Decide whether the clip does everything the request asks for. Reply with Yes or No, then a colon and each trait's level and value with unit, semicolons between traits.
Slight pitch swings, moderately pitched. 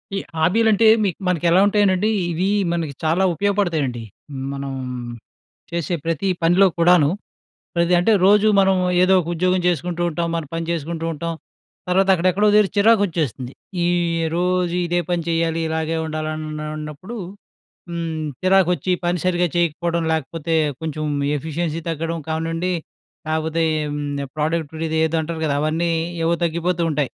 Yes: narrow, 2.3 semitones; medium, 170 Hz